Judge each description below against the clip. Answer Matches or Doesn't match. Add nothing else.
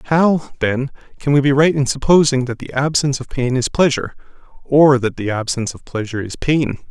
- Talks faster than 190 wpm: Matches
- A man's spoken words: Matches